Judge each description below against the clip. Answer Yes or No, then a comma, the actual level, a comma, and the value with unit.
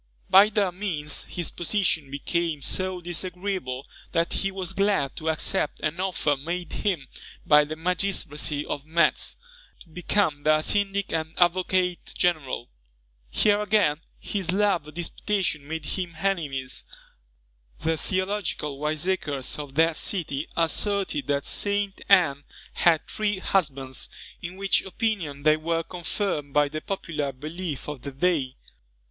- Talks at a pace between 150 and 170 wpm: No, slow, 135 wpm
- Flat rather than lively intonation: No, average, 4.3 semitones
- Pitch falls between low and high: Yes, medium, 170 Hz